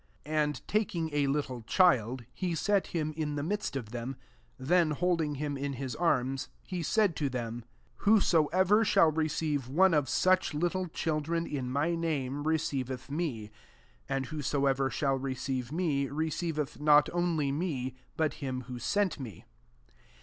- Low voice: No, medium, 150 Hz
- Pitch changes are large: No, average, 3.9 semitones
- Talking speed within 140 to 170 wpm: Yes, average, 160 wpm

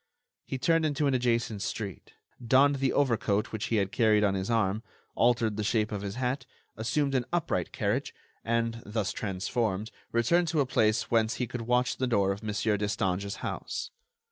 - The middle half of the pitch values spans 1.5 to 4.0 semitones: Yes, average, 3.2 semitones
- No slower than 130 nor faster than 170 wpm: No, average, 180 wpm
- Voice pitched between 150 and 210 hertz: No, low, 115 Hz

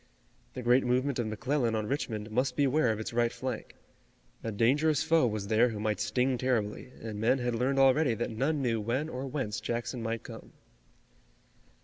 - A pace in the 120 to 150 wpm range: No, average, 180 wpm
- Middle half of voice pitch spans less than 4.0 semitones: Yes, average, 3.1 semitones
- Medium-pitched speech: No, low, 120 Hz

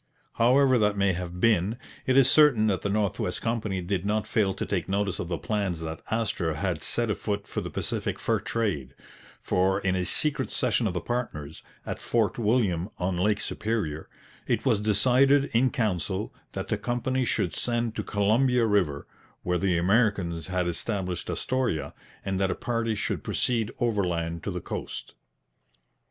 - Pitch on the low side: Yes, low, 105 Hz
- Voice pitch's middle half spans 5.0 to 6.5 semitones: No, average, 4.4 semitones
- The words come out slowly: No, average, 170 wpm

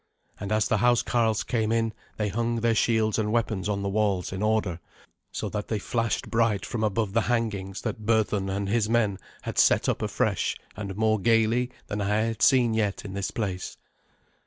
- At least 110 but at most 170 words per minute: No, average, 190 wpm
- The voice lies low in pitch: Yes, low, 110 Hz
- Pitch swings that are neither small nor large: No, narrow, 2.2 semitones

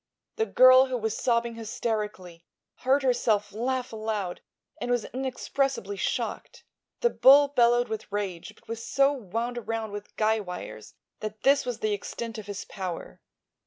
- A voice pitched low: No, high, 225 Hz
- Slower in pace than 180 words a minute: Yes, average, 155 wpm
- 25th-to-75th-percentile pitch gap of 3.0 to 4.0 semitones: Yes, average, 3.6 semitones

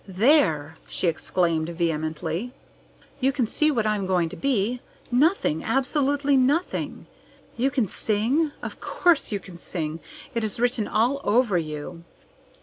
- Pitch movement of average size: No, wide, 7.6 semitones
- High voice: Yes, high, 215 Hz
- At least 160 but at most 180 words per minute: No, average, 140 wpm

